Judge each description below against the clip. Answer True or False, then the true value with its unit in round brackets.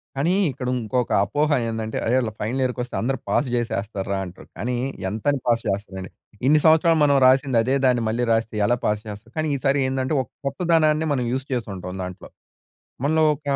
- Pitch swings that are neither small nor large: True (4.5 semitones)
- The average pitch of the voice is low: True (125 Hz)